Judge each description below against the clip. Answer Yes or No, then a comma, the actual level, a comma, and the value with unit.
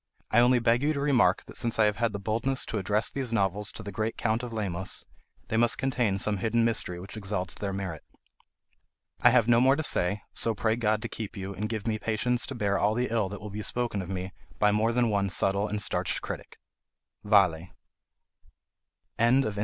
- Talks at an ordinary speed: No, fast, 215 wpm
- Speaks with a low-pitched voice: Yes, low, 110 Hz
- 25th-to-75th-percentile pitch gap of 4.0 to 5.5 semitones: No, average, 2.9 semitones